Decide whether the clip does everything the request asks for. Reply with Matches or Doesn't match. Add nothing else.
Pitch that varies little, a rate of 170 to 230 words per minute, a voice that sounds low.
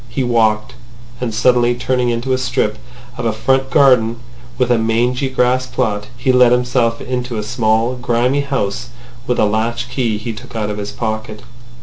Matches